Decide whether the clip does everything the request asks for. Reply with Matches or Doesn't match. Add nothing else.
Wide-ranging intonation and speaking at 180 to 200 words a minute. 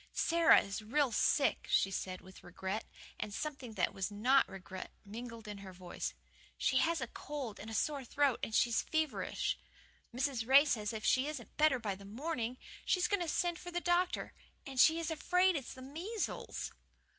Matches